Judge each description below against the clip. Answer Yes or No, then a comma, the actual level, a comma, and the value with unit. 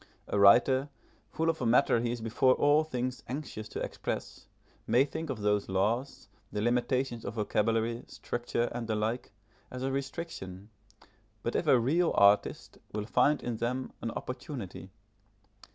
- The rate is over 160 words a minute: No, average, 155 wpm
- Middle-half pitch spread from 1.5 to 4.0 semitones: Yes, average, 3.6 semitones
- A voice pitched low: Yes, low, 120 Hz